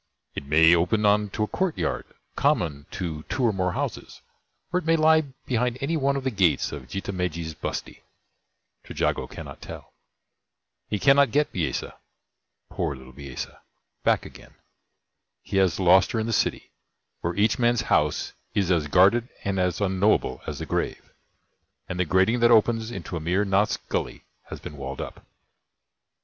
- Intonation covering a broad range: Yes, wide, 5.7 semitones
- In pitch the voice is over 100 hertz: No, very low, 95 Hz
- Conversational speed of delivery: Yes, average, 165 wpm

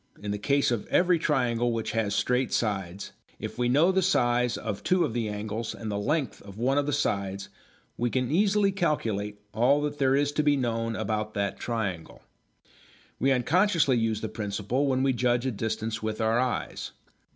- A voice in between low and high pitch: No, low, 120 Hz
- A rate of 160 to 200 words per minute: Yes, average, 190 wpm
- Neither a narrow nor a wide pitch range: Yes, average, 4.6 semitones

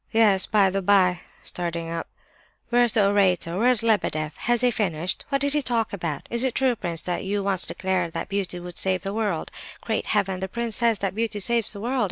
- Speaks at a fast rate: Yes, fast, 215 wpm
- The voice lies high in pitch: Yes, high, 200 Hz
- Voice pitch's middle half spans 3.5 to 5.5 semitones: Yes, average, 4.1 semitones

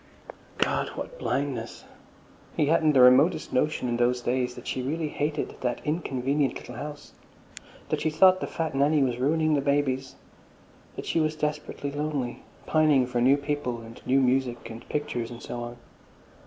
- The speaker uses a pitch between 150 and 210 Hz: No, medium, 140 Hz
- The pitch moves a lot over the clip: No, average, 3.3 semitones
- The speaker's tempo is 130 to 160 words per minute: No, average, 170 wpm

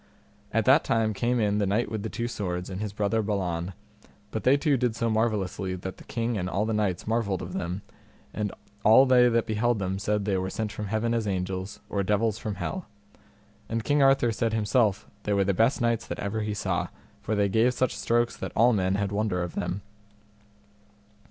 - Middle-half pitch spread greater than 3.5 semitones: No, average, 2.9 semitones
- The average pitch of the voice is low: Yes, low, 105 Hz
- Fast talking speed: Yes, fast, 210 wpm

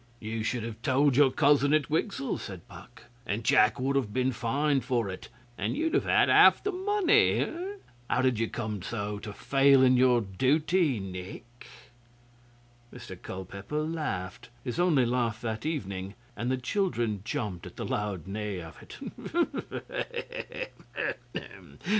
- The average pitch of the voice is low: Yes, low, 125 Hz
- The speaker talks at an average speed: Yes, average, 145 wpm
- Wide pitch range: Yes, wide, 5.8 semitones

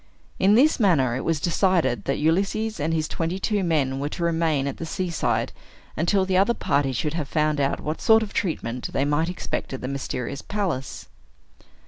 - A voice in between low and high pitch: Yes, medium, 160 Hz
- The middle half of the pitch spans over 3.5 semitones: Yes, average, 5.1 semitones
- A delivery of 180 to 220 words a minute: Yes, average, 190 wpm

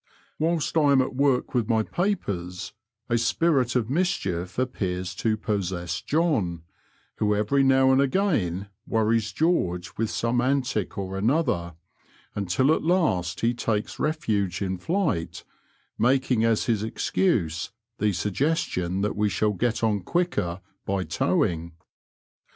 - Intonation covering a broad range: Yes, wide, 6.4 semitones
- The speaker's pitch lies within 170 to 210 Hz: No, low, 110 Hz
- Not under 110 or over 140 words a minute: Yes, slow, 135 wpm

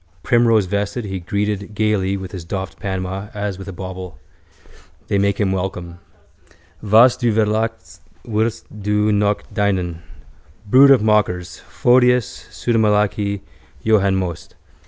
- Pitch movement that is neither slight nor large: No, narrow, 2.3 semitones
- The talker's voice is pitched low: Yes, low, 100 Hz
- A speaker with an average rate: No, slow, 120 wpm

